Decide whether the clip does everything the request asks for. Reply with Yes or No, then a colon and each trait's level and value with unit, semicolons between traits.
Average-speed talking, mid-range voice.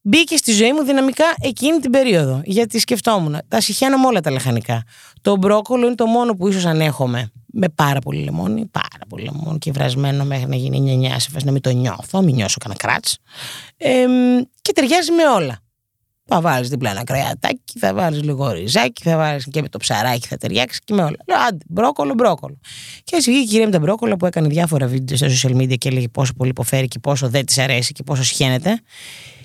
No: fast, 205 wpm; medium, 150 Hz